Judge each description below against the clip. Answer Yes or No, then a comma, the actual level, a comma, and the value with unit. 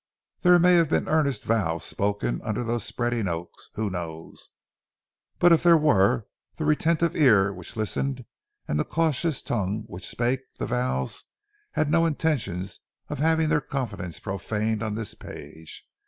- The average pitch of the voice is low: Yes, low, 115 Hz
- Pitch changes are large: Yes, wide, 8.1 semitones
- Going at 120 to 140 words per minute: No, average, 150 wpm